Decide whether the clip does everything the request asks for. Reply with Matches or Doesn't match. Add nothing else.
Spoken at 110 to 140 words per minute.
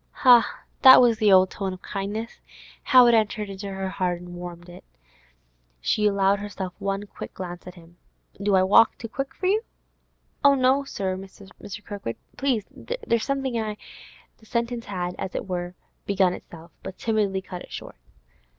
Doesn't match